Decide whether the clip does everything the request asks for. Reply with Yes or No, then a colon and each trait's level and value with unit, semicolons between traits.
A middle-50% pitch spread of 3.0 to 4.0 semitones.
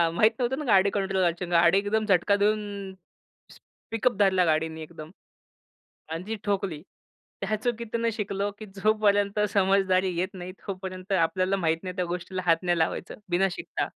No: narrow, 2.4 semitones